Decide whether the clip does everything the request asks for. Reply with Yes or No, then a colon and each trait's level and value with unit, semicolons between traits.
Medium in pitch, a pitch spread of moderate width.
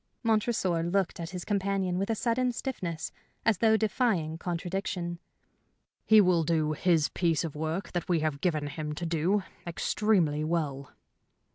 Yes: medium, 175 Hz; average, 3.9 semitones